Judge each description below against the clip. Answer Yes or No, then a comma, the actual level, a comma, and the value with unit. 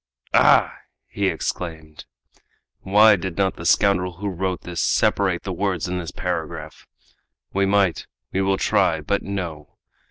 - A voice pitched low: Yes, very low, 90 Hz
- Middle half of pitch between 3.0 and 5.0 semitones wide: No, narrow, 2.6 semitones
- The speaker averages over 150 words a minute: No, average, 145 wpm